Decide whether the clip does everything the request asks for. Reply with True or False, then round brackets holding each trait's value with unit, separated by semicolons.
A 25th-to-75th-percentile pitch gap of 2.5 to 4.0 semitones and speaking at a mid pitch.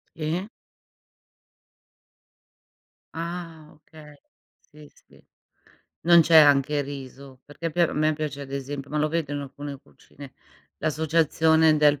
False (2.0 semitones; 150 Hz)